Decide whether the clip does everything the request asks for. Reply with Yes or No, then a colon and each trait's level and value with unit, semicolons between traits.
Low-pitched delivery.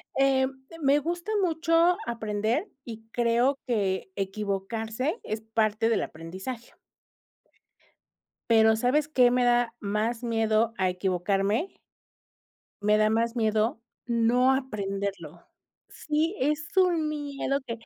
No: high, 230 Hz